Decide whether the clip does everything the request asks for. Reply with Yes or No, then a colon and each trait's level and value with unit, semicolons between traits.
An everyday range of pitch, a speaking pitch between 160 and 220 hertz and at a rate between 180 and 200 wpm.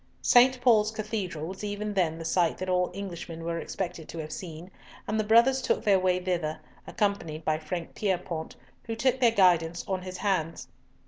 Yes: average, 4.1 semitones; medium, 185 Hz; average, 185 wpm